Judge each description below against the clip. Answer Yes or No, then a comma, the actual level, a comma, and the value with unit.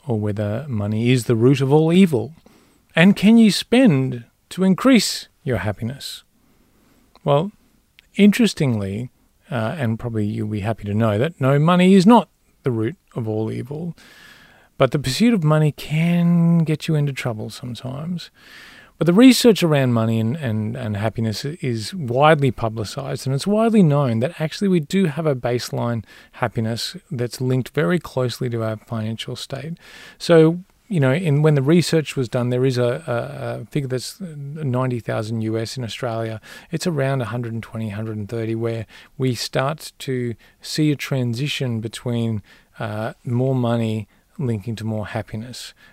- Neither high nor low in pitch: No, low, 130 Hz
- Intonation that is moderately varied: No, wide, 5.8 semitones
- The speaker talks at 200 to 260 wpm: No, average, 155 wpm